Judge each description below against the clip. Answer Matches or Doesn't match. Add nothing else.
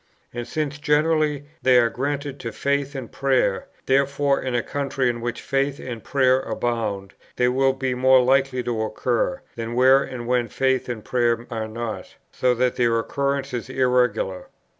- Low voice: Matches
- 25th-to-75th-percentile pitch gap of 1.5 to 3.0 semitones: Matches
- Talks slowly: Doesn't match